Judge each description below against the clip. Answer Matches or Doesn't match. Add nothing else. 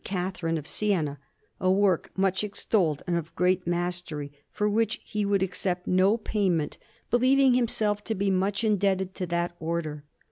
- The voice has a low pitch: Doesn't match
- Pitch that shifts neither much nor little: Matches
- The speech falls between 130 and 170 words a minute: Matches